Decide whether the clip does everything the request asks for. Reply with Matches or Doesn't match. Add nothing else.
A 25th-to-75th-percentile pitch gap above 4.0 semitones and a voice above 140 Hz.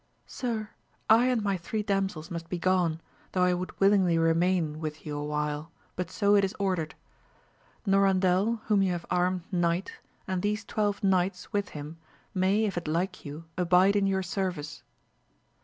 Doesn't match